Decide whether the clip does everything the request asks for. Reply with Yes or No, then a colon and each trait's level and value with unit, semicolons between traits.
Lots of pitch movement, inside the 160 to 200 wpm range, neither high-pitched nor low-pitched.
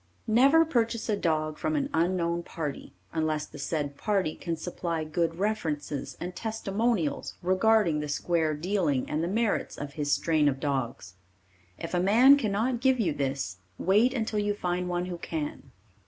Yes: wide, 5.7 semitones; average, 165 wpm; medium, 175 Hz